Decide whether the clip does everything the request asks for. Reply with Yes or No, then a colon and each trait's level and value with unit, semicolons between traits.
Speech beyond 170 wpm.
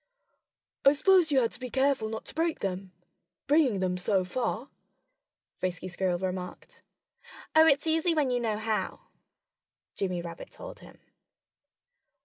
No: average, 140 wpm